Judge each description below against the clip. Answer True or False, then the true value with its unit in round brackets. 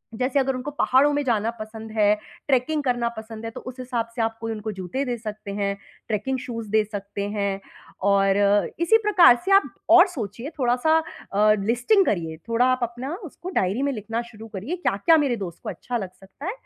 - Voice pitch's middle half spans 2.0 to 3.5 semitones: False (4.2 semitones)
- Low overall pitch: False (230 Hz)